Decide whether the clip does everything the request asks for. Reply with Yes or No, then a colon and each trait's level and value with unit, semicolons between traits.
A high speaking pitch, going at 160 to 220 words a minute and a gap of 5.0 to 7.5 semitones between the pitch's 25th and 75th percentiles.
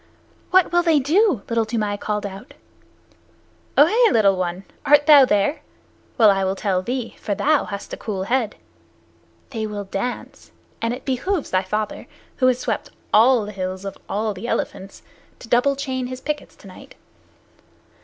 Yes: high, 230 Hz; average, 165 wpm; wide, 5.4 semitones